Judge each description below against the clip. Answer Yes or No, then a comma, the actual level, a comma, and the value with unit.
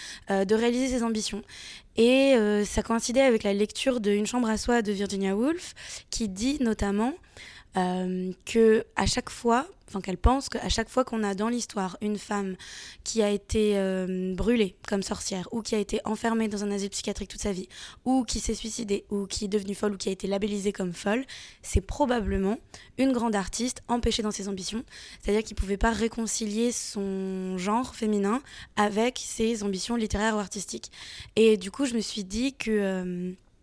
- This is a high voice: Yes, high, 215 Hz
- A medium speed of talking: Yes, average, 190 wpm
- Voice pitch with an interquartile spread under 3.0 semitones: Yes, narrow, 2.5 semitones